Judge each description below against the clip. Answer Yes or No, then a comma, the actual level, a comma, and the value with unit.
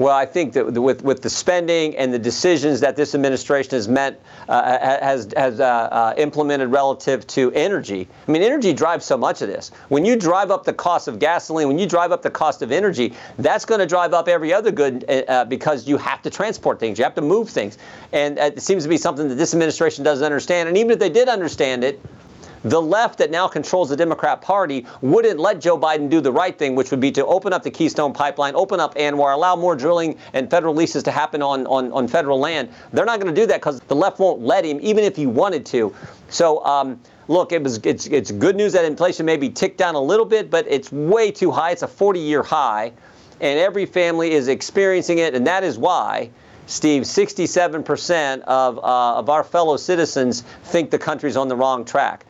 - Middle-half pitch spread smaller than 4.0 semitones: No, average, 4.4 semitones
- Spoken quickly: Yes, fast, 225 wpm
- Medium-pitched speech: Yes, medium, 150 Hz